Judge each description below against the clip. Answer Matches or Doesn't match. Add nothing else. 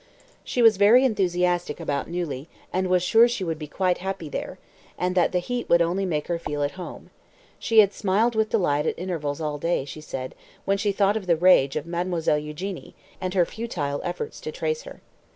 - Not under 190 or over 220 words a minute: Matches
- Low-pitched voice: Doesn't match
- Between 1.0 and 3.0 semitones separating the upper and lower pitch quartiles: Doesn't match